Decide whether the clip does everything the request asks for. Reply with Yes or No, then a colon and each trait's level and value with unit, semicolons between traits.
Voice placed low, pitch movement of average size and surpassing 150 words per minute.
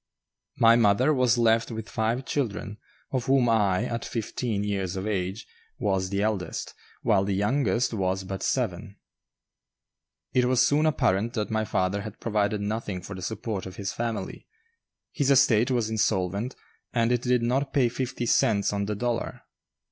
Yes: low, 110 Hz; average, 3.4 semitones; average, 165 wpm